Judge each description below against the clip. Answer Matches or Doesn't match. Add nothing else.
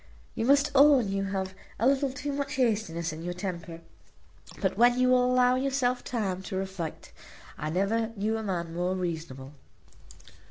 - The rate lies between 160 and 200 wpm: Matches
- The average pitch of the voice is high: Matches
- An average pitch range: Doesn't match